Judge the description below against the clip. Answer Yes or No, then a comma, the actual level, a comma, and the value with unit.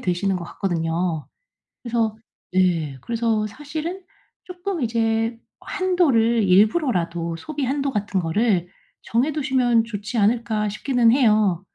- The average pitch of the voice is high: Yes, high, 225 Hz